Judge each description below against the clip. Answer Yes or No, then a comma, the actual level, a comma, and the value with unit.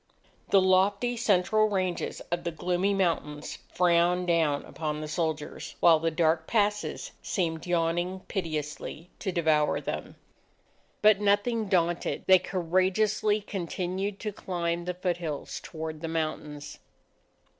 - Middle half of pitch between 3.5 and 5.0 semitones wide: No, average, 3.1 semitones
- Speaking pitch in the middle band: Yes, medium, 175 Hz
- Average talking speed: No, slow, 125 wpm